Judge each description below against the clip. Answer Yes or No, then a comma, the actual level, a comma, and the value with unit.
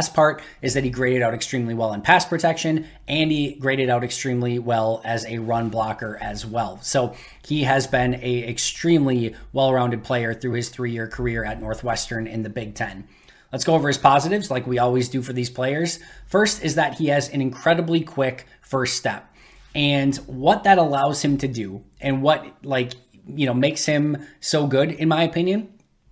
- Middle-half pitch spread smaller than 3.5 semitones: No, average, 4.2 semitones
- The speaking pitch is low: Yes, low, 130 Hz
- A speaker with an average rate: Yes, average, 195 wpm